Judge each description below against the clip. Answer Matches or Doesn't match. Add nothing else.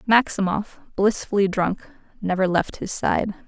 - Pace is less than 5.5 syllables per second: Matches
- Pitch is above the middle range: Matches